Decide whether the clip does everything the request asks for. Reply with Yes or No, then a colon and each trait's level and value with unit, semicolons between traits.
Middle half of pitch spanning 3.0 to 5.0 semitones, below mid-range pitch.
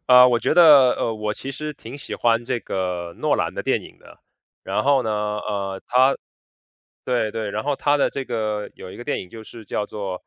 Yes: average, 3.7 semitones; low, 115 Hz